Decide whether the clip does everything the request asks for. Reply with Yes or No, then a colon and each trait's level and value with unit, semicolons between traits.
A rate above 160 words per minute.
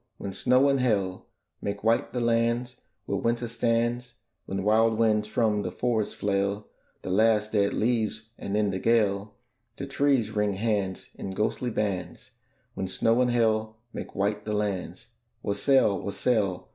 No: average, 155 wpm